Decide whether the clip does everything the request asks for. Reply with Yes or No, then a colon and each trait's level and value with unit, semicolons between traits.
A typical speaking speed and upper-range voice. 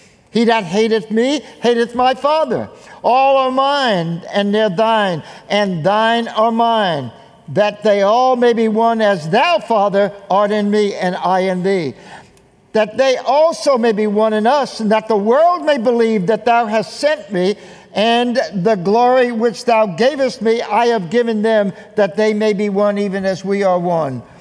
Yes: average, 180 wpm; high, 220 Hz